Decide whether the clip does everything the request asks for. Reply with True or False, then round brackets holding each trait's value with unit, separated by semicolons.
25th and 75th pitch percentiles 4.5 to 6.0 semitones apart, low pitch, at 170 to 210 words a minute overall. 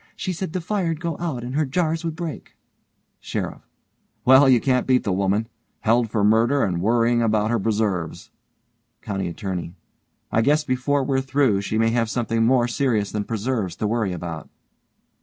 True (4.8 semitones; 120 Hz; 175 wpm)